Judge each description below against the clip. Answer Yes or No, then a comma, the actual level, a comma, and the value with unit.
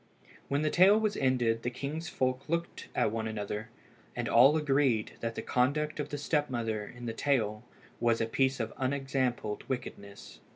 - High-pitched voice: No, low, 130 Hz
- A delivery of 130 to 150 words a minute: No, average, 175 wpm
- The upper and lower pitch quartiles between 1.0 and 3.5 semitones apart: No, average, 4.1 semitones